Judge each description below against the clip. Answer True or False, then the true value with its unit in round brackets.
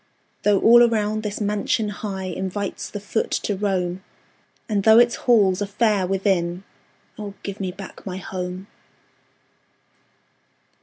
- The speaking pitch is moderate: False (200 Hz)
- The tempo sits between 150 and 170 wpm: False (135 wpm)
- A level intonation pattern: True (2.0 semitones)